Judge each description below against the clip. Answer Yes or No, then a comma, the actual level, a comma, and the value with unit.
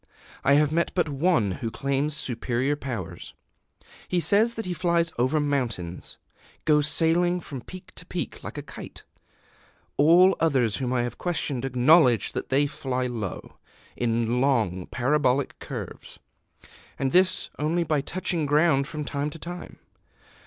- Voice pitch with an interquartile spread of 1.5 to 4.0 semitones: No, average, 5.1 semitones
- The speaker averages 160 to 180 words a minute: No, average, 145 wpm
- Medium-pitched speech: Yes, medium, 145 Hz